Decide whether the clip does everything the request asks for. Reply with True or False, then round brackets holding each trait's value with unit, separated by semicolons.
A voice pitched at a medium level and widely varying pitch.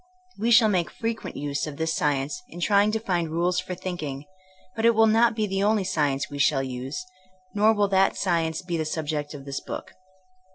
True (175 Hz; 6.1 semitones)